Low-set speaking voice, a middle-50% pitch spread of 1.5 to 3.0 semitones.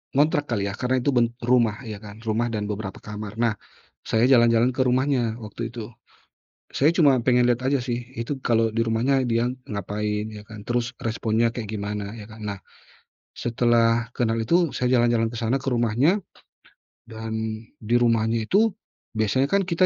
Yes: low, 115 Hz; narrow, 2.4 semitones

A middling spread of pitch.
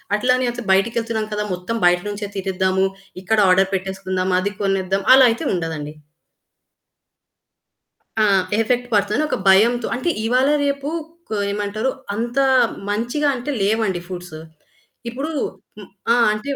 Yes: average, 4.1 semitones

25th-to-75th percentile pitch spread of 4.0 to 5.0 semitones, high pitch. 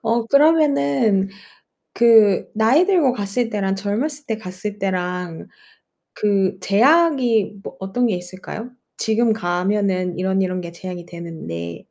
Yes: average, 4.3 semitones; high, 200 Hz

